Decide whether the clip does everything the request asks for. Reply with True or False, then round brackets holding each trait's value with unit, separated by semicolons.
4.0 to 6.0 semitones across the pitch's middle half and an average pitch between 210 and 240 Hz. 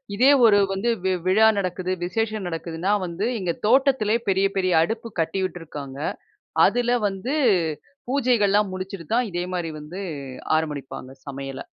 False (4.7 semitones; 190 Hz)